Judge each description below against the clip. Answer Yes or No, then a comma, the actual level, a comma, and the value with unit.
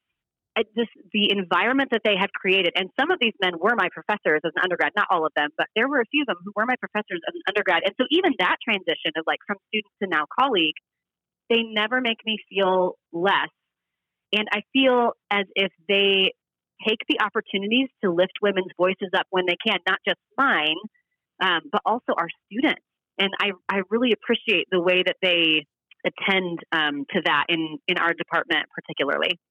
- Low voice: No, high, 195 Hz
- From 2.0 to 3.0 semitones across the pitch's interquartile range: No, average, 3.8 semitones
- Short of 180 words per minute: No, average, 200 wpm